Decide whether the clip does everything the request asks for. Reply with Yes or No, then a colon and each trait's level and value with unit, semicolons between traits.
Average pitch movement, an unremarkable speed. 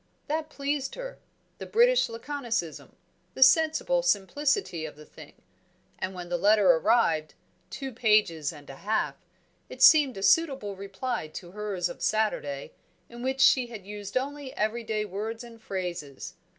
No: wide, 6.5 semitones; average, 150 wpm